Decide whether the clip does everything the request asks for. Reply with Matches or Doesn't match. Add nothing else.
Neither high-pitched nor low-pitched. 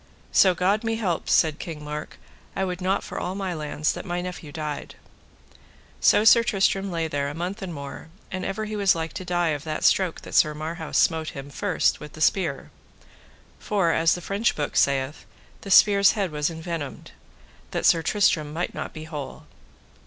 Matches